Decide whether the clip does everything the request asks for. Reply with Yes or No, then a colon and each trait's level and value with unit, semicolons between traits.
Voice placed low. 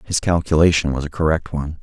Yes: very low, 80 Hz